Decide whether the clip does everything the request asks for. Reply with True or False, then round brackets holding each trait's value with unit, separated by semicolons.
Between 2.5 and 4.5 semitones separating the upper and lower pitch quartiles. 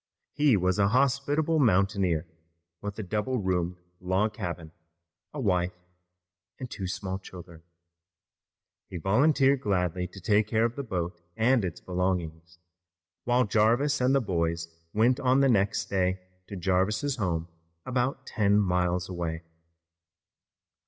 False (5.5 semitones)